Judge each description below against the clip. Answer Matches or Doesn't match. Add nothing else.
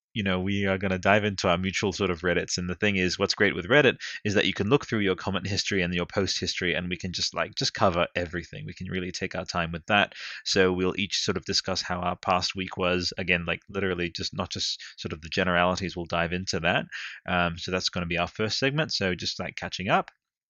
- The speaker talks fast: Matches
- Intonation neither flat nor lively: Doesn't match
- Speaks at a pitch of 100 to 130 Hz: Doesn't match